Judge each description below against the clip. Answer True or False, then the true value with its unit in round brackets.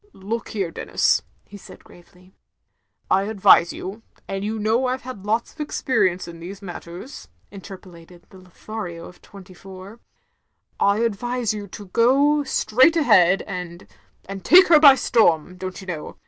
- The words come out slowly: False (175 wpm)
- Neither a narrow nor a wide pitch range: True (4.2 semitones)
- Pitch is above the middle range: True (200 Hz)